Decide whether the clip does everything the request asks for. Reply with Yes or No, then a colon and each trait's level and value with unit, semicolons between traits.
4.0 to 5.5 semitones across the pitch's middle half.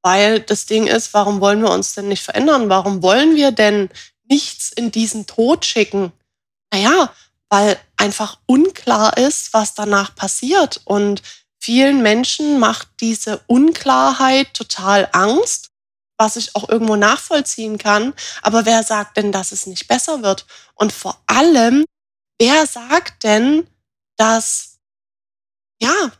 Yes: average, 4.9 semitones